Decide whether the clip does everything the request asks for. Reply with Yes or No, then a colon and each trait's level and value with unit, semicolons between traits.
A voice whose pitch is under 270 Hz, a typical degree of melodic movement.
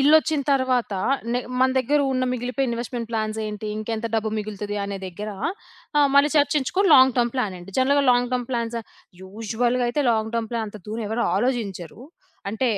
Yes: high, 235 Hz; average, 3.2 semitones